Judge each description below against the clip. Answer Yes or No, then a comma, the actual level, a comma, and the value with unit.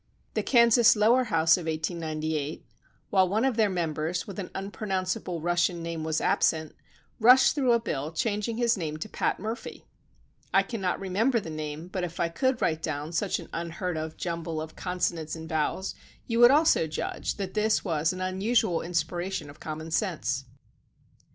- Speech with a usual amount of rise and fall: Yes, average, 4.9 semitones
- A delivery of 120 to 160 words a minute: No, average, 175 wpm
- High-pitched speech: No, medium, 175 Hz